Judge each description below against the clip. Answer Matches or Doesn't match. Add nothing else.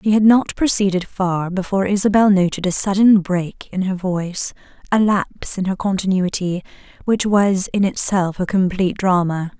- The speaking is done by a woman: Matches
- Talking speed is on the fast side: Doesn't match